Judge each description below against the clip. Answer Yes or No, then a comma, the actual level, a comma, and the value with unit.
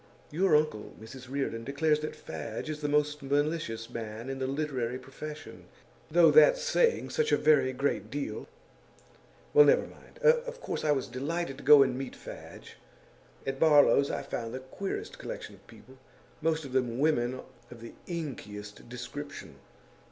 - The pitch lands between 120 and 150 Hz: Yes, medium, 140 Hz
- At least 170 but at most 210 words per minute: No, average, 160 wpm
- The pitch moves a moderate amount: Yes, average, 3.4 semitones